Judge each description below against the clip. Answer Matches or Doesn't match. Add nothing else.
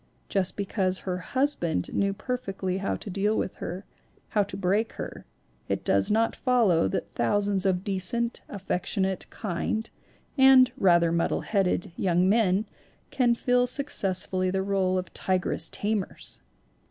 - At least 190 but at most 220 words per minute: Doesn't match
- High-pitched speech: Matches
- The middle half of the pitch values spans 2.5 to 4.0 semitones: Matches